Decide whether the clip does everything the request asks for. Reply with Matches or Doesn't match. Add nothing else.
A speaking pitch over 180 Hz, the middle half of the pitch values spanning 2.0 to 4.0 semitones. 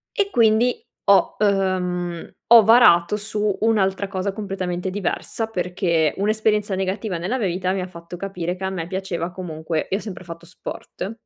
Matches